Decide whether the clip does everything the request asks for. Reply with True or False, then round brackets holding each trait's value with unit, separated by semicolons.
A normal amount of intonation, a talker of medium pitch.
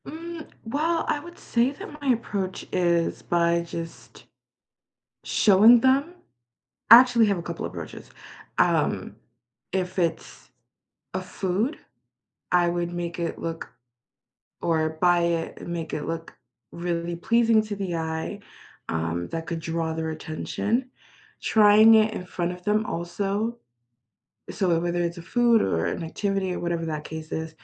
True (4.8 semitones; 175 Hz)